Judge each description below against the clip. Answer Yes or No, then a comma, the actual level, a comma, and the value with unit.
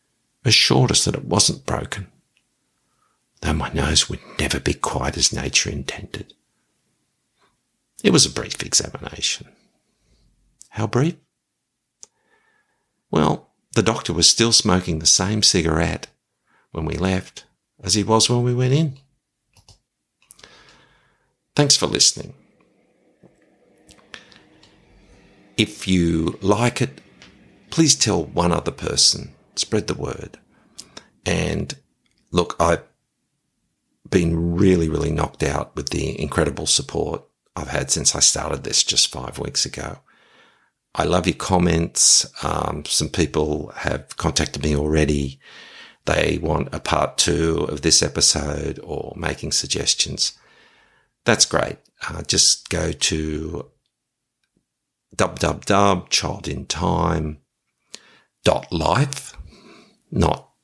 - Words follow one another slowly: Yes, slow, 115 wpm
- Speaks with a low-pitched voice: Yes, very low, 90 Hz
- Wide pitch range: Yes, wide, 7.5 semitones